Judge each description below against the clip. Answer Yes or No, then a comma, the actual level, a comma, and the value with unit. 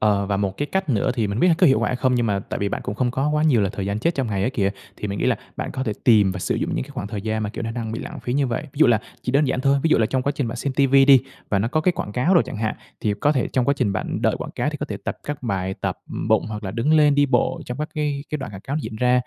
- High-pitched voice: No, low, 125 Hz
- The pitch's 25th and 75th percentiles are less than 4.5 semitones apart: No, average, 5.1 semitones